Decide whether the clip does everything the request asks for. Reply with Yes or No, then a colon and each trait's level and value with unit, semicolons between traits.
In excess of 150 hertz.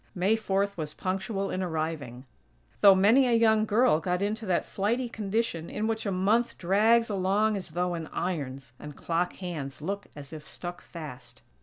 Yes: high, 190 Hz